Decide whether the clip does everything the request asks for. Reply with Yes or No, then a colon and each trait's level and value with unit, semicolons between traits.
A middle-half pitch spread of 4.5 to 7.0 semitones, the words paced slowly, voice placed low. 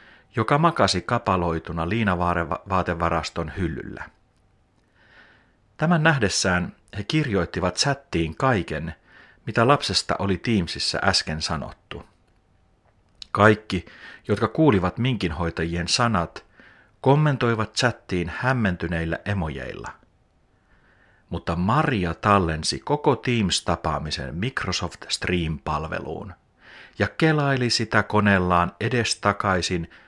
Yes: average, 4.9 semitones; slow, 75 wpm; very low, 95 Hz